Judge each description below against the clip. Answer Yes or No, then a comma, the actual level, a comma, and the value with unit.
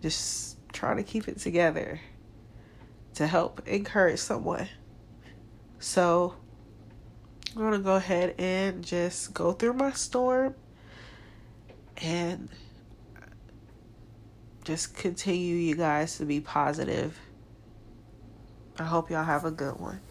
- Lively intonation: Yes, wide, 7.4 semitones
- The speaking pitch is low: Yes, low, 120 Hz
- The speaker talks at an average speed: No, slow, 105 wpm